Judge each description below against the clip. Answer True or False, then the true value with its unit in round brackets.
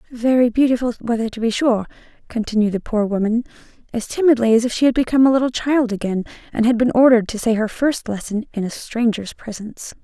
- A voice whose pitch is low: False (235 Hz)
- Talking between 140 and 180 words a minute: False (205 wpm)